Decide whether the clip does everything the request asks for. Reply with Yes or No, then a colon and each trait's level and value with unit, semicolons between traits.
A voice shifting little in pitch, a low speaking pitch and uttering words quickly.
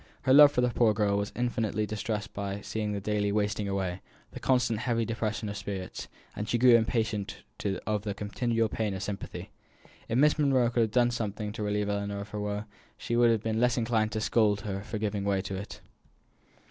Yes: narrow, 2.3 semitones; low, 105 Hz; fast, 210 wpm